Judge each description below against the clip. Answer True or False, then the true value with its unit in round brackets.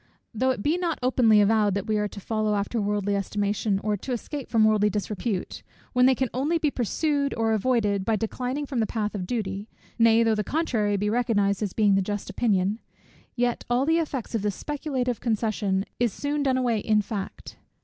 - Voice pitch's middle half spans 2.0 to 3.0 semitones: False (3.5 semitones)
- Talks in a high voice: True (220 Hz)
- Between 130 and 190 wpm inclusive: False (200 wpm)